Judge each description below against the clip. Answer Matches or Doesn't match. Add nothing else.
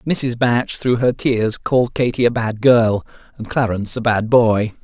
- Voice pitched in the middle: Doesn't match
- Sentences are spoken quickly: Doesn't match